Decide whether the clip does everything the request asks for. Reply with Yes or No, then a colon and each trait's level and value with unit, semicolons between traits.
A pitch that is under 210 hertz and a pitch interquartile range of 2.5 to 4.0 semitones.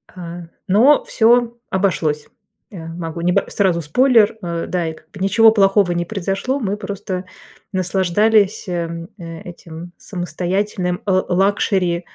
Yes: medium, 185 Hz; average, 3.0 semitones